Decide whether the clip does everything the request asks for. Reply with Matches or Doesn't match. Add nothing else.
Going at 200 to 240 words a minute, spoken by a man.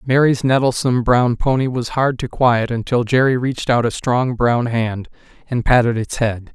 Doesn't match